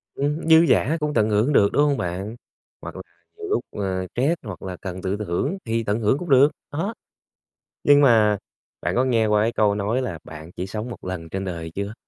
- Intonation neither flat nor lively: No, wide, 6.5 semitones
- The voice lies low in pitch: Yes, low, 110 Hz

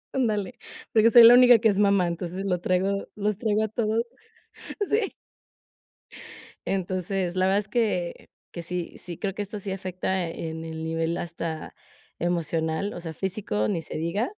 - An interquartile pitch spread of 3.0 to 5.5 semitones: Yes, average, 3.7 semitones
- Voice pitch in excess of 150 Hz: Yes, high, 190 Hz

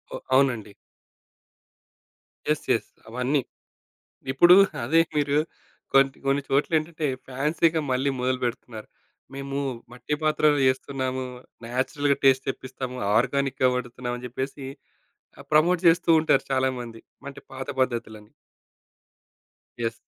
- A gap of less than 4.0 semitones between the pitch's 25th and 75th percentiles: Yes, narrow, 2.5 semitones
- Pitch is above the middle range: No, low, 135 Hz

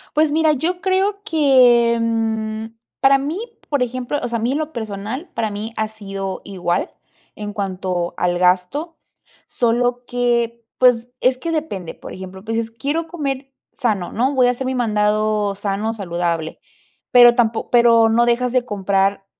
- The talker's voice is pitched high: Yes, high, 230 Hz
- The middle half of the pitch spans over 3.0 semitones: Yes, average, 4.0 semitones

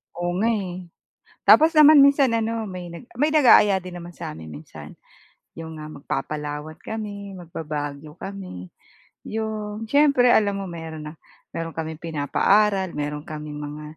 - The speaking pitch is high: No, medium, 175 Hz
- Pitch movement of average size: No, wide, 6.0 semitones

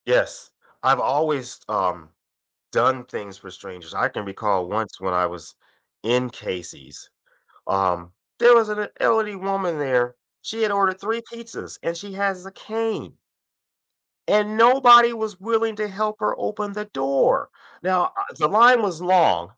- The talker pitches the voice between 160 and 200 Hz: Yes, high, 190 Hz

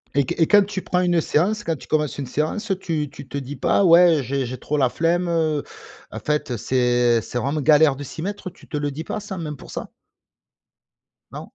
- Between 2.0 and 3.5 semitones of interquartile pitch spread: No, average, 3.9 semitones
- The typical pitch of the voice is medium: Yes, medium, 150 Hz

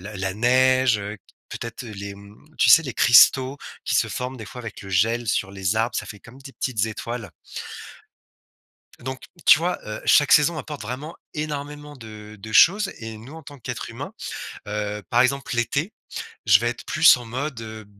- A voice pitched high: No, low, 120 Hz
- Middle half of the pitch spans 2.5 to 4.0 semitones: No, average, 4.5 semitones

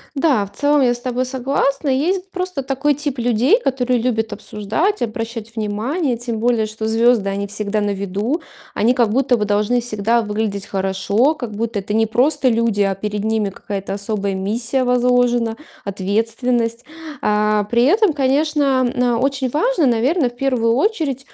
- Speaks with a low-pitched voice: No, high, 235 Hz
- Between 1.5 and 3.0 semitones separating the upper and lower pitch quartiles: No, average, 4.1 semitones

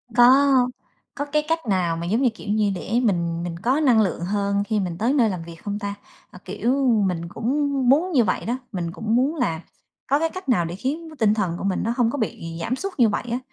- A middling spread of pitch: No, wide, 6.3 semitones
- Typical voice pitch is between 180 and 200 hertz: No, high, 220 Hz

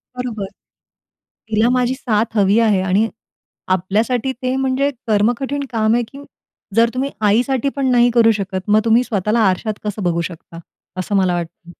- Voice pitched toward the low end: No, high, 225 Hz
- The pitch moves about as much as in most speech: Yes, average, 4.0 semitones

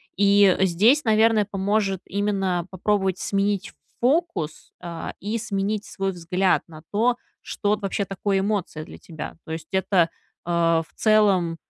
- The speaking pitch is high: Yes, high, 195 Hz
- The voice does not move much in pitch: No, average, 3.0 semitones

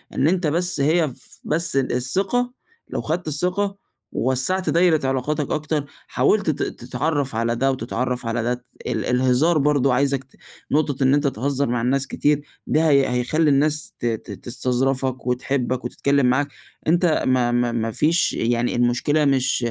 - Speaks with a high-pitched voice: No, low, 135 Hz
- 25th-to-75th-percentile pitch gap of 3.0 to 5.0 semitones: Yes, average, 3.6 semitones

